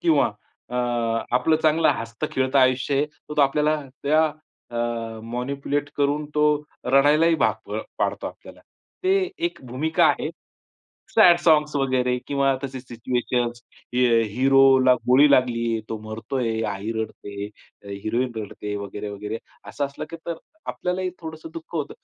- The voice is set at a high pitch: No, low, 130 Hz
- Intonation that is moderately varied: Yes, average, 4.3 semitones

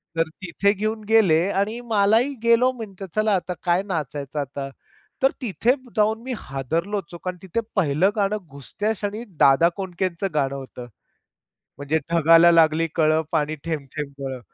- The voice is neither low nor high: Yes, medium, 175 Hz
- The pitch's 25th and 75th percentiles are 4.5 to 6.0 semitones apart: Yes, wide, 5.4 semitones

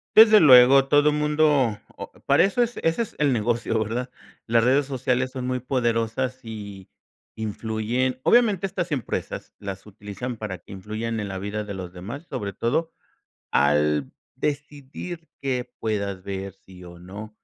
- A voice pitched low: Yes, low, 120 Hz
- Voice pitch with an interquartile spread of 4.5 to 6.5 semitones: Yes, wide, 5.4 semitones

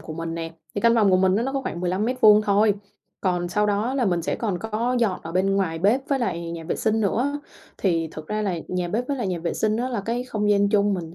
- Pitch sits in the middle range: No, high, 205 Hz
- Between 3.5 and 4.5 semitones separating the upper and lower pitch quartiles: Yes, average, 4.2 semitones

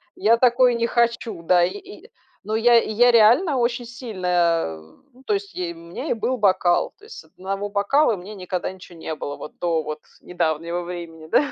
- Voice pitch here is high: Yes, high, 205 Hz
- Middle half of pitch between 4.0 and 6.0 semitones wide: Yes, wide, 5.5 semitones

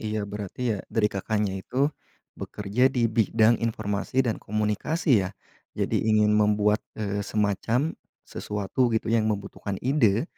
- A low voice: Yes, low, 110 Hz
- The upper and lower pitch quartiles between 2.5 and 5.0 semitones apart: No, narrow, 2.0 semitones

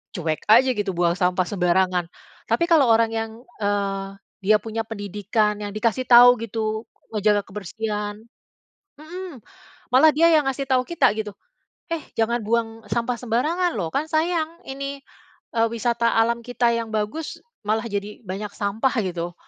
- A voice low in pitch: No, high, 225 Hz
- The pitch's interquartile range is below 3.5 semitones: No, average, 3.9 semitones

